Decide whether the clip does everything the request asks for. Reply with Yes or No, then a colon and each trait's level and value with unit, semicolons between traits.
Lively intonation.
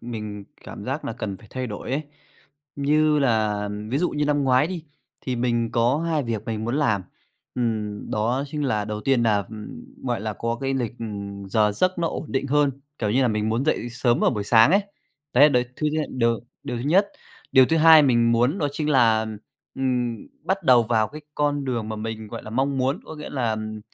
No: average, 4.5 semitones